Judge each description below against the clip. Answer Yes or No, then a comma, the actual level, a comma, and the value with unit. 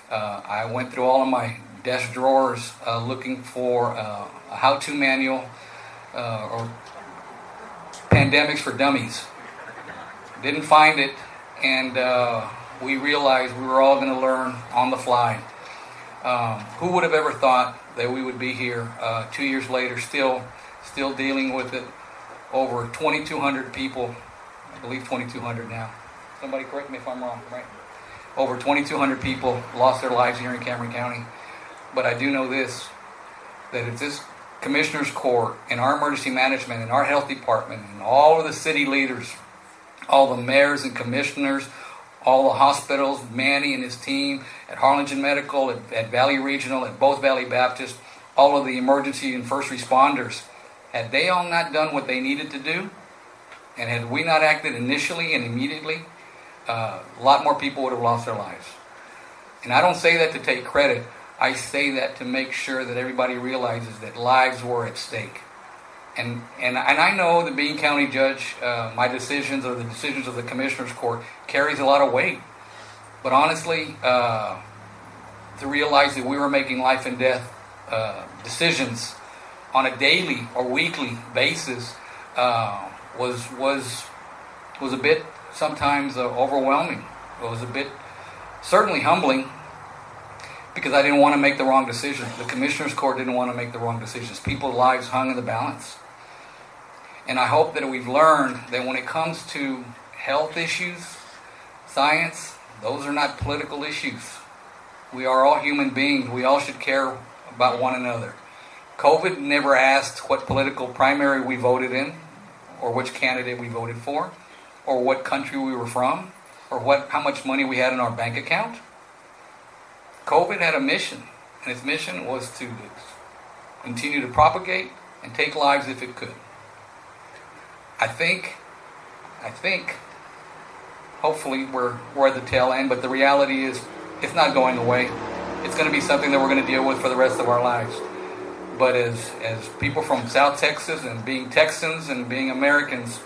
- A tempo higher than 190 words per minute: No, average, 165 wpm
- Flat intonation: Yes, narrow, 2.2 semitones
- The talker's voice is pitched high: No, low, 130 Hz